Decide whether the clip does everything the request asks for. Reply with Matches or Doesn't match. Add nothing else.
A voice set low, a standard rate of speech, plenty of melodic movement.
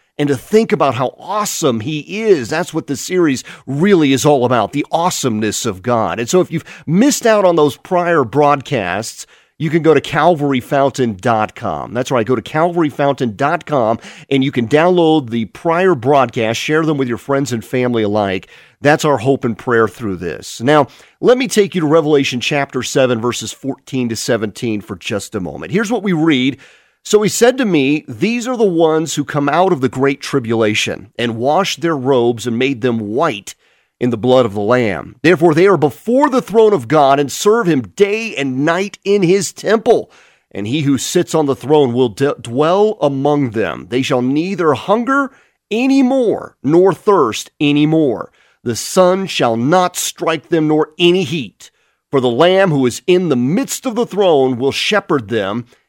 Doesn't match